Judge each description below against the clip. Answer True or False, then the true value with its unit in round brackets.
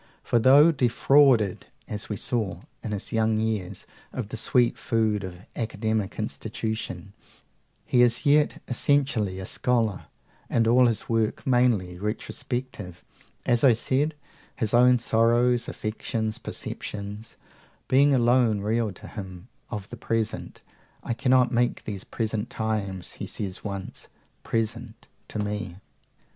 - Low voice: True (115 Hz)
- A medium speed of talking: False (130 wpm)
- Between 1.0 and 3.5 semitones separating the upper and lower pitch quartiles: True (2.8 semitones)